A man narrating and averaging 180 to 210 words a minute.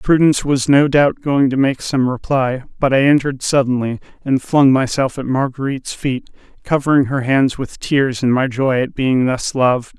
Yes: male; average, 185 wpm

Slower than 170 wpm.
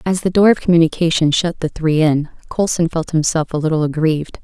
No: fast, 205 wpm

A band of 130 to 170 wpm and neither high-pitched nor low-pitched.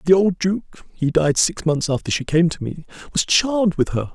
No: fast, 205 wpm; medium, 170 Hz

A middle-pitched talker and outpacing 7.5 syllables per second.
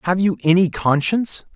No: medium, 180 Hz; 5.4 syllables/s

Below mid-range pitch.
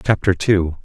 Yes: very low, 90 Hz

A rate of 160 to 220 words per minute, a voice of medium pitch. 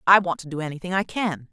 No: fast, 275 wpm; medium, 175 Hz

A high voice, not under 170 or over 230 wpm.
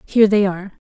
Yes: high, 200 Hz; fast, 205 wpm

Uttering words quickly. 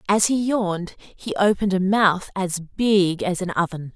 No: average, 180 wpm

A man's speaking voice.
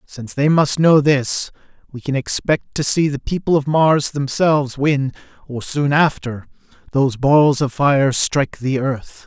Yes: male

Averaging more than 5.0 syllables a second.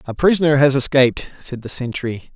Yes: 5.6 syllables/s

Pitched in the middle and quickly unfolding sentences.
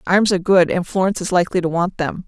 Yes: medium, 180 Hz; fast, 265 wpm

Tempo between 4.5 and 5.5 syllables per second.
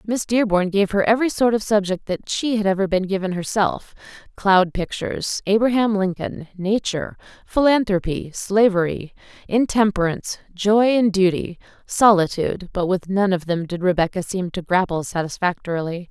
Yes: 5.1 syllables/s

